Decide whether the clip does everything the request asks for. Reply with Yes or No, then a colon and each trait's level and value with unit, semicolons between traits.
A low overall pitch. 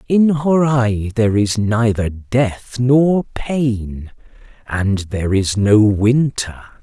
Yes: low, 115 Hz